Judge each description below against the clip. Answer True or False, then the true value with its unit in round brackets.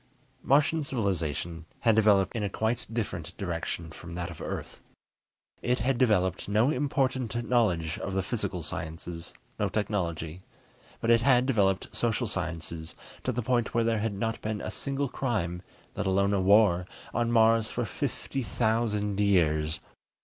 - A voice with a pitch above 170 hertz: False (105 Hz)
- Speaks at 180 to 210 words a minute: False (155 wpm)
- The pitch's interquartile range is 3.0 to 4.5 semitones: False (5.0 semitones)